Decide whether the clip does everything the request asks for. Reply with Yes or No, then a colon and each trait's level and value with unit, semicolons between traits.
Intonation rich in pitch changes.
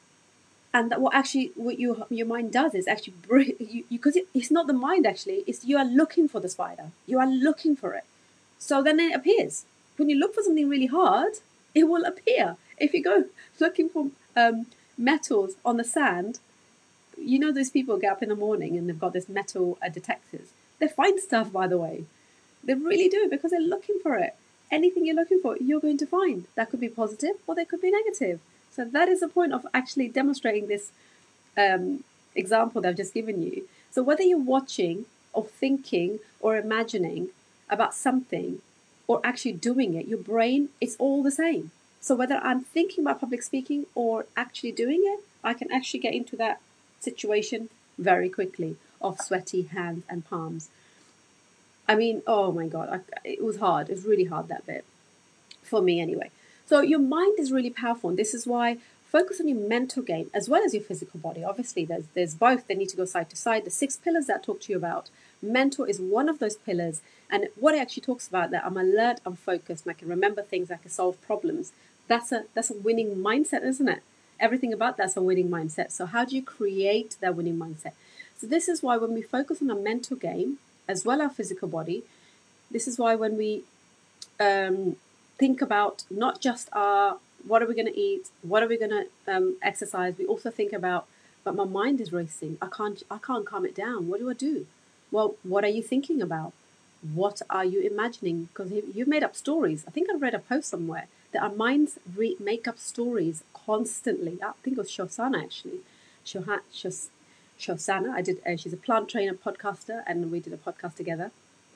Yes: wide, 6.8 semitones